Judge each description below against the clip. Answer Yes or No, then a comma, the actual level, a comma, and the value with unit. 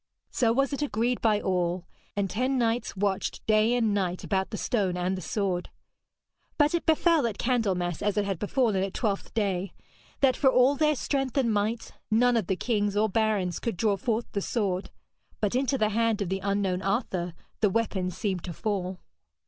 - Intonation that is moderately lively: Yes, average, 3.9 semitones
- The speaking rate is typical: Yes, average, 190 wpm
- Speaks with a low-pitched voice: No, high, 210 Hz